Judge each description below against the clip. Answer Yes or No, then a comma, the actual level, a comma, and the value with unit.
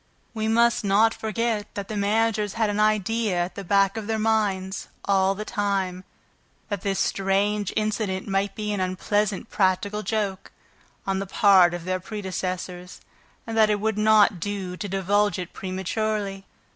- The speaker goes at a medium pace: Yes, average, 160 wpm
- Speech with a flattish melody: Yes, narrow, 2.1 semitones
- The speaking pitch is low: No, high, 200 Hz